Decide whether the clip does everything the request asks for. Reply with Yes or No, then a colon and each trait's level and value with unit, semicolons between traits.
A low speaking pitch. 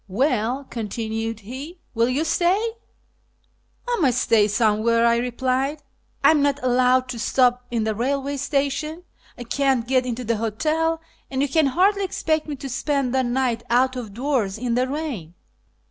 No: very high, 255 Hz